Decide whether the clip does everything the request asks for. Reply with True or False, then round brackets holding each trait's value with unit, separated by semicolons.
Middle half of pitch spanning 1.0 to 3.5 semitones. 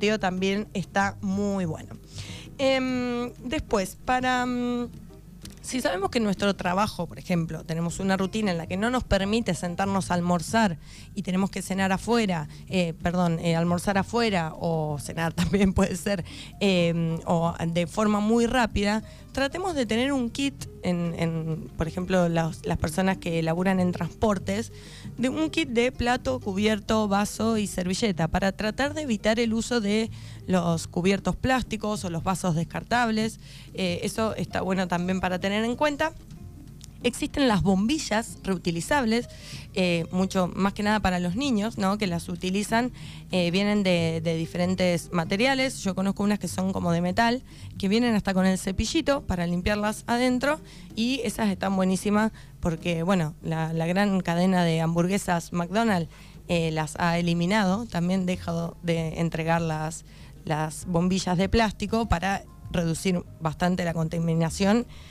False (4.3 semitones)